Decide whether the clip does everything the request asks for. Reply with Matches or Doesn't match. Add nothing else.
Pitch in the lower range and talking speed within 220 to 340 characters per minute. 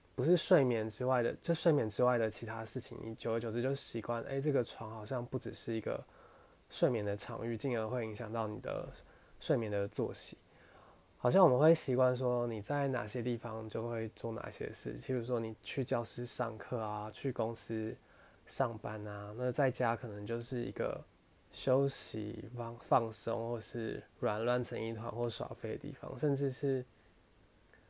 Matches